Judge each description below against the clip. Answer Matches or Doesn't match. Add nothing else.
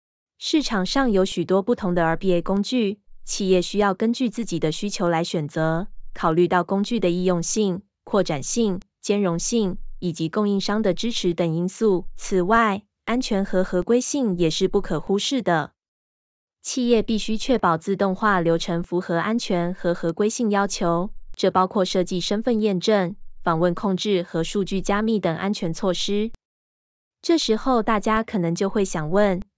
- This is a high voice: Matches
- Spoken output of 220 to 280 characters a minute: Matches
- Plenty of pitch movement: Doesn't match